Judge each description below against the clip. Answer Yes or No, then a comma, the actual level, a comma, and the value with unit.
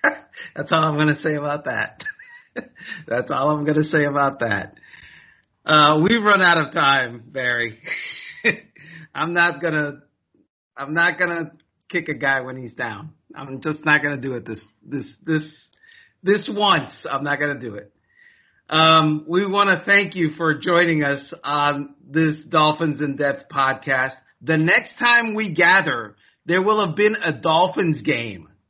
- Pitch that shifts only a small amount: No, average, 3.6 semitones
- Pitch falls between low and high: Yes, medium, 155 Hz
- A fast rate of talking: No, average, 170 wpm